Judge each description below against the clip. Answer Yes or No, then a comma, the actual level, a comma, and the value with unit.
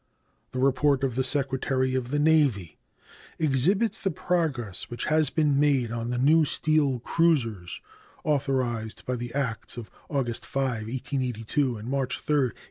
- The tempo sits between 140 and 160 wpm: Yes, average, 150 wpm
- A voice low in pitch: Yes, low, 130 Hz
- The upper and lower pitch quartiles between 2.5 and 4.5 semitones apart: Yes, average, 3.5 semitones